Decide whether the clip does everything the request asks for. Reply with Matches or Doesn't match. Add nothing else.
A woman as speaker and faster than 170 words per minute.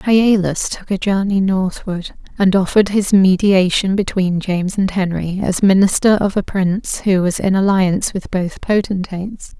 Doesn't match